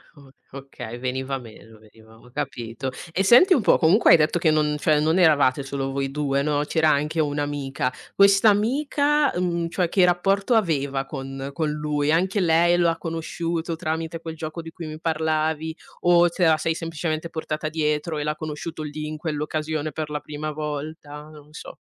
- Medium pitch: Yes, medium, 155 Hz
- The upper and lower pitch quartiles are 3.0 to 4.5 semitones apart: No, narrow, 2.5 semitones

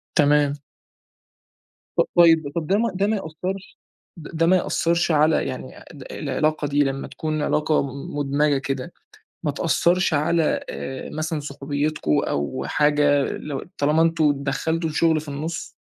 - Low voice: No, medium, 150 Hz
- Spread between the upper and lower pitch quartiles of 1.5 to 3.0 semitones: Yes, narrow, 2.4 semitones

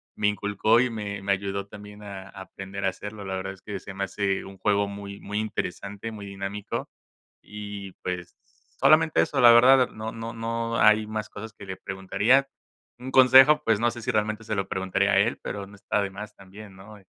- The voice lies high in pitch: No, low, 105 Hz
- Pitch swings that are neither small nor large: No, narrow, 2.3 semitones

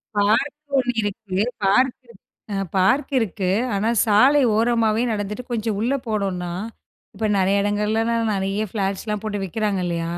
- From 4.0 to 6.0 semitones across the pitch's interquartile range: No, average, 2.8 semitones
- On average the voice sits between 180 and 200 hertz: No, high, 215 Hz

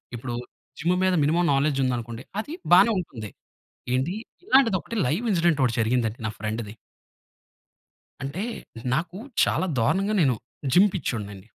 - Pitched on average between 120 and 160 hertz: Yes, medium, 140 Hz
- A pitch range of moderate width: No, wide, 7.6 semitones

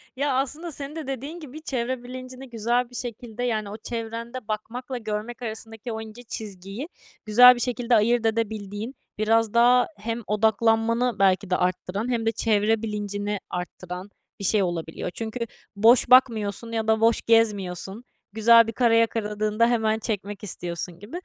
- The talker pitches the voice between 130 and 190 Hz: No, high, 225 Hz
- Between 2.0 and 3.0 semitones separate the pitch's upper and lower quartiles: Yes, narrow, 2.6 semitones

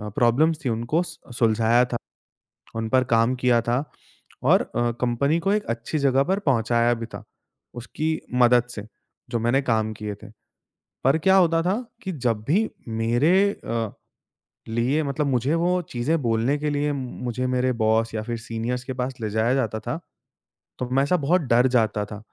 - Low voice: Yes, low, 120 Hz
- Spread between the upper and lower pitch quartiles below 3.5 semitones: No, average, 3.8 semitones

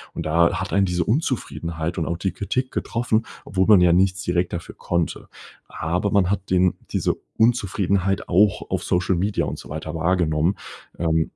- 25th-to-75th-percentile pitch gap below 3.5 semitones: Yes, average, 2.9 semitones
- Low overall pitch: Yes, very low, 90 Hz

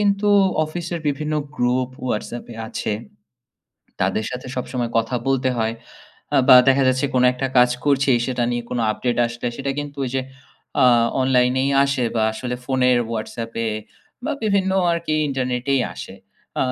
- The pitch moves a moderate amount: No, narrow, 2.2 semitones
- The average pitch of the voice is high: No, low, 130 Hz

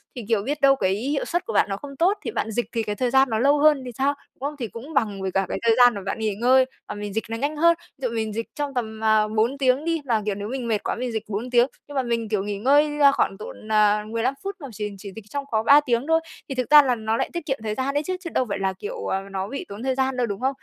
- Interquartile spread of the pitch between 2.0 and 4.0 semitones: No, average, 4.5 semitones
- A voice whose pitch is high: Yes, high, 240 Hz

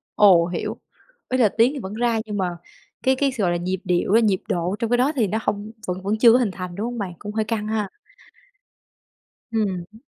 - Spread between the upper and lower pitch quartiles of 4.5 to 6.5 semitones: No, average, 3.7 semitones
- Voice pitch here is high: Yes, high, 210 Hz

